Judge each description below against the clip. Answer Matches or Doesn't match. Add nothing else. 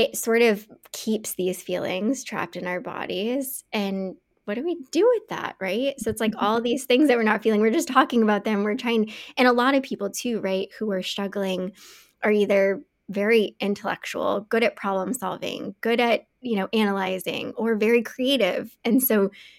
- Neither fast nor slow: Matches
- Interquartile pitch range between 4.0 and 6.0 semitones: Doesn't match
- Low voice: Doesn't match